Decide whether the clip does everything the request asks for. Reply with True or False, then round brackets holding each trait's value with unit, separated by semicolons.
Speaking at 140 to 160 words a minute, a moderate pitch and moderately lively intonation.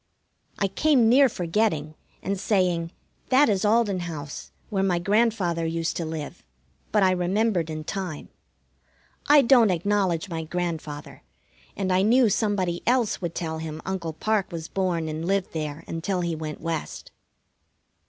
True (150 wpm; 180 Hz; 4.1 semitones)